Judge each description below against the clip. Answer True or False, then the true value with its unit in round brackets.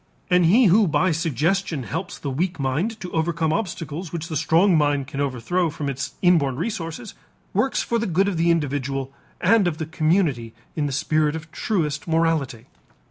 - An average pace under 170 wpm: False (180 wpm)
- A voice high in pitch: False (165 Hz)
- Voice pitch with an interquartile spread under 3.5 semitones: False (3.8 semitones)